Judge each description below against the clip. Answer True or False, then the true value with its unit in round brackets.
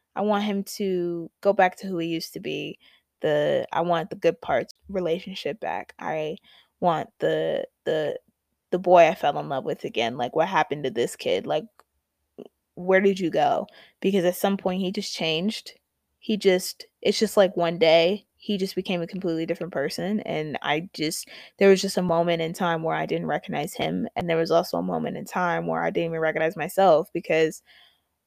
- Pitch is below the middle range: False (185 Hz)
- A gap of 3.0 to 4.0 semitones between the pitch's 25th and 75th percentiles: True (3.5 semitones)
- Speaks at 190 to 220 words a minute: True (200 wpm)